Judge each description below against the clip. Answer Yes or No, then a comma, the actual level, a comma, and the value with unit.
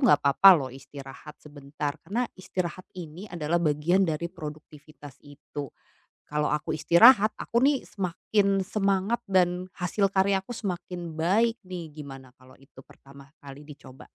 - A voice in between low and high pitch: Yes, medium, 170 Hz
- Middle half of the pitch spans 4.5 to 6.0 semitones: Yes, average, 4.9 semitones